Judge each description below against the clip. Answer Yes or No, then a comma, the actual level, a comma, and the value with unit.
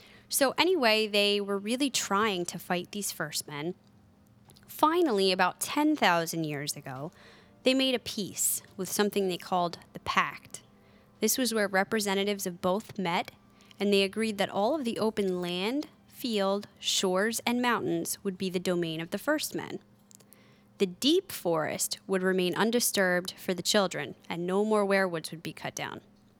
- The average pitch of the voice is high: Yes, high, 195 Hz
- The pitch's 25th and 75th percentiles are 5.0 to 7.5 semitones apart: No, average, 3.6 semitones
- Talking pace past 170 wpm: No, average, 160 wpm